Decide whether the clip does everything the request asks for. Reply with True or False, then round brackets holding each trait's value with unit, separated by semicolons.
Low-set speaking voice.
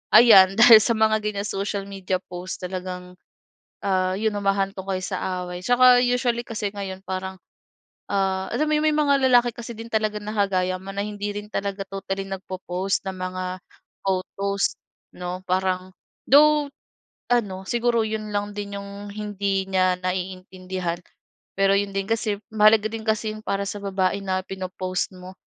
False (195 Hz)